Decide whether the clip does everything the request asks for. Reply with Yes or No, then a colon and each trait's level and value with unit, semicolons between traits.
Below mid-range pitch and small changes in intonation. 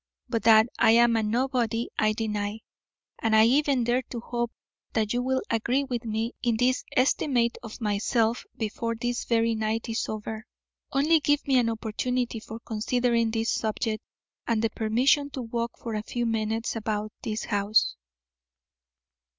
No: high, 230 Hz; narrow, 1.9 semitones